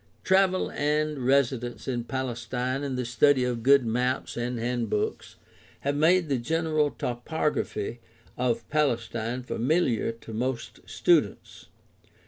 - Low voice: Yes, low, 125 Hz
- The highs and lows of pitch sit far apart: No, average, 3.5 semitones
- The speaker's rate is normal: No, slow, 115 wpm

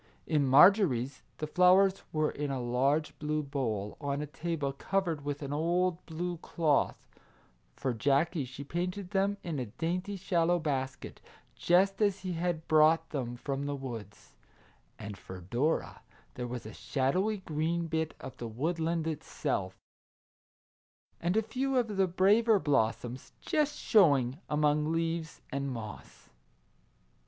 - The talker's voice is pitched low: No, medium, 155 Hz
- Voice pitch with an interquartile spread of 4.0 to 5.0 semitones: Yes, average, 4.7 semitones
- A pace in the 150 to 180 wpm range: No, average, 140 wpm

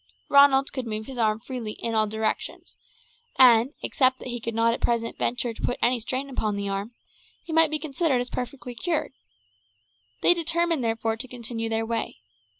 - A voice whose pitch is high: Yes, high, 240 Hz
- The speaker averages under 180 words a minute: No, average, 185 wpm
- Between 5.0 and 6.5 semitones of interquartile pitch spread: No, average, 3.0 semitones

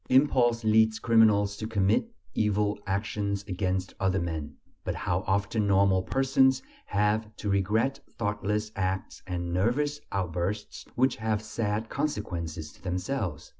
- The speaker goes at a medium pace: No, slow, 130 wpm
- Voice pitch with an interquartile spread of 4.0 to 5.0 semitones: No, average, 2.8 semitones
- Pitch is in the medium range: No, low, 105 Hz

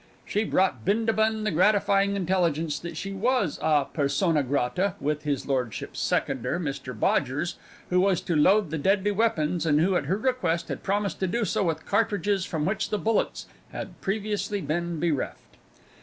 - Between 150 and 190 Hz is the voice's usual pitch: Yes, medium, 185 Hz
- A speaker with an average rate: Yes, average, 170 wpm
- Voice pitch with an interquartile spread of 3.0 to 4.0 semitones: No, average, 5.1 semitones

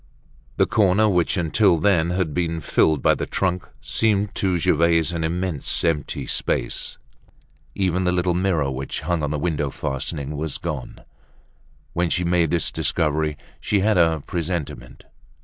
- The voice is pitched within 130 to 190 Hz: No, very low, 85 Hz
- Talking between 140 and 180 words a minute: Yes, average, 150 wpm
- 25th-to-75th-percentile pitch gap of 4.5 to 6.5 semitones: No, average, 3.0 semitones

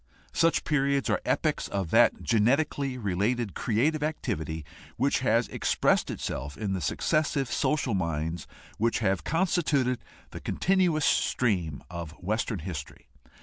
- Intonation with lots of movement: Yes, wide, 7.6 semitones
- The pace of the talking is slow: Yes, slow, 125 wpm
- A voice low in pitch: Yes, low, 115 Hz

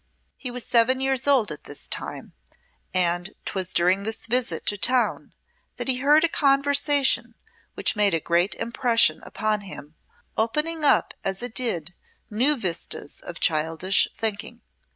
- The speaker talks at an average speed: Yes, average, 150 wpm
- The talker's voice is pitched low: No, high, 225 Hz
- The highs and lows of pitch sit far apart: Yes, wide, 6.1 semitones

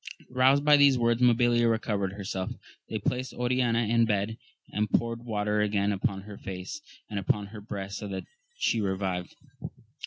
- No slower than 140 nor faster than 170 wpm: Yes, average, 160 wpm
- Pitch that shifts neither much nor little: Yes, average, 3.1 semitones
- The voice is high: No, low, 105 Hz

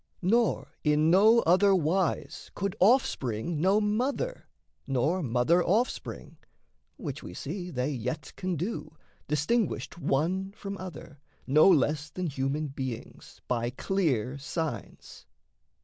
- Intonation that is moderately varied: No, wide, 5.7 semitones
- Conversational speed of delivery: No, slow, 115 wpm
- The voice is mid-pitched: Yes, medium, 165 Hz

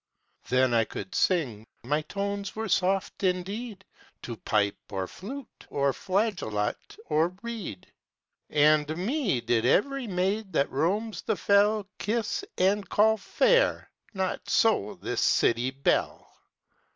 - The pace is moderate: No, slow, 125 wpm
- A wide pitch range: Yes, wide, 7.4 semitones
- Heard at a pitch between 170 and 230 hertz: Yes, medium, 185 Hz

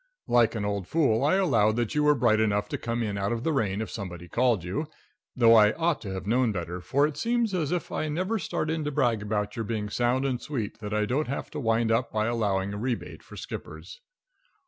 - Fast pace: Yes, fast, 240 wpm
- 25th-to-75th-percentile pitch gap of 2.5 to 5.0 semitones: No, wide, 5.6 semitones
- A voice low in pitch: Yes, low, 115 Hz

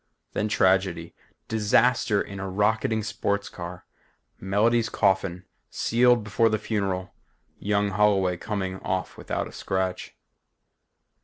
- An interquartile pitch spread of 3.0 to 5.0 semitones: No, narrow, 2.4 semitones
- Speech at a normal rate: No, slow, 110 wpm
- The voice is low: Yes, low, 100 Hz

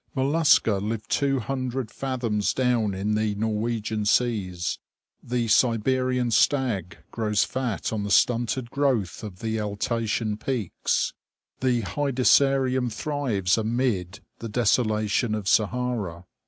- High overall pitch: No, low, 115 Hz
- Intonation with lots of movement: No, average, 3.4 semitones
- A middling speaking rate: No, slow, 110 wpm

